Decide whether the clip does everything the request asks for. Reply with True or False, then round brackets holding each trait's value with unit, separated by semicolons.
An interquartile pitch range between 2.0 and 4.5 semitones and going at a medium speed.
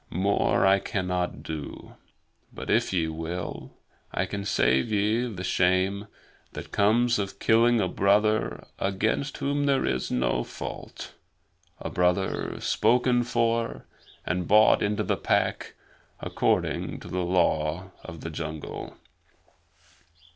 False (3.9 semitones; 125 wpm)